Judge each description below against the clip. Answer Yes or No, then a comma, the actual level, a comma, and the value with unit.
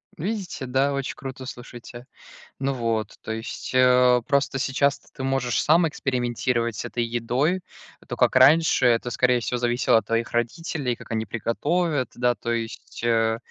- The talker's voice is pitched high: No, low, 125 Hz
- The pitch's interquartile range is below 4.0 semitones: Yes, average, 2.7 semitones